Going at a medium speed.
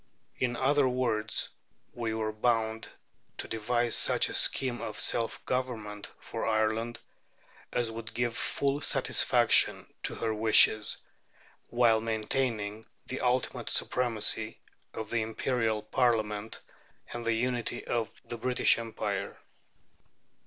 No: slow, 115 wpm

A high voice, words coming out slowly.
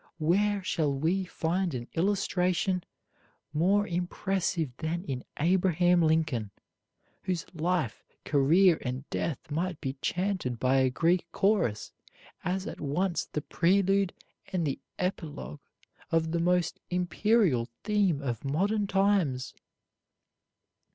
No: medium, 170 Hz; slow, 115 wpm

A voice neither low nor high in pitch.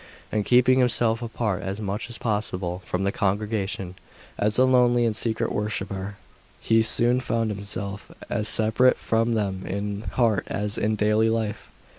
No: low, 110 Hz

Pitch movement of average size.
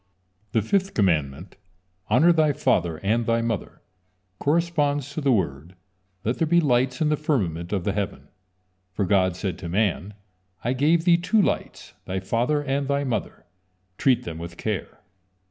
No: wide, 7.9 semitones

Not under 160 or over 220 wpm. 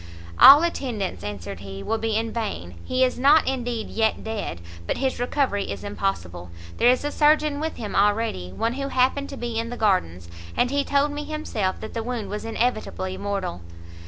Yes: average, 190 wpm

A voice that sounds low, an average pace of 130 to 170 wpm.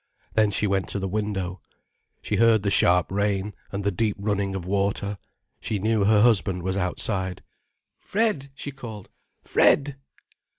Yes: low, 100 Hz; average, 155 wpm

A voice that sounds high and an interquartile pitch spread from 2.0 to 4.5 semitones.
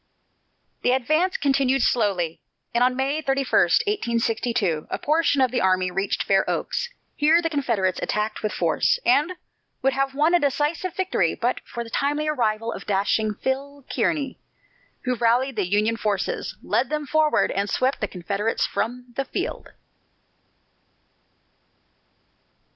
No: very high, 250 Hz; average, 5.1 semitones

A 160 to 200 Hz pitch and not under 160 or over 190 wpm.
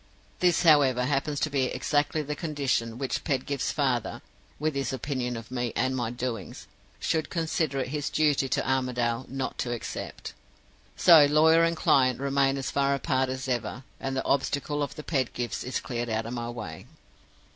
No: low, 135 Hz; average, 175 wpm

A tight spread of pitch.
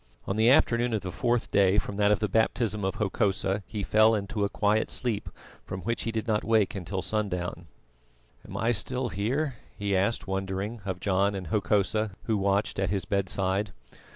Yes: narrow, 2.3 semitones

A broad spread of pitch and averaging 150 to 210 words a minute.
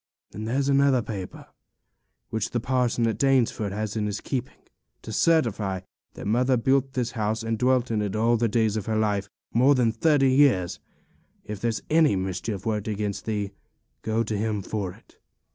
No: average, 3.4 semitones; average, 180 wpm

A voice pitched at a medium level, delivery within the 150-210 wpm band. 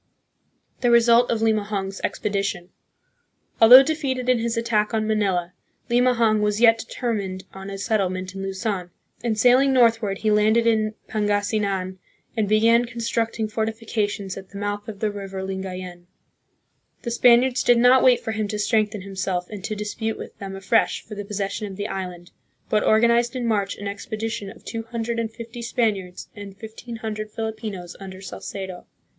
No: high, 215 Hz; average, 170 wpm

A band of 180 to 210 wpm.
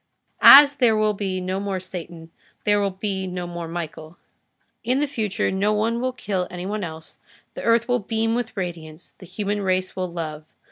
Yes: average, 190 wpm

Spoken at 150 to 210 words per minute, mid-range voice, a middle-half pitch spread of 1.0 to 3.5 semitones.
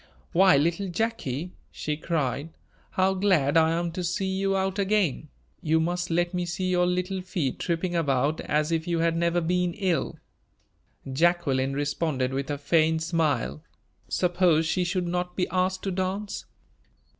Yes: average, 155 wpm; medium, 175 Hz; narrow, 2.6 semitones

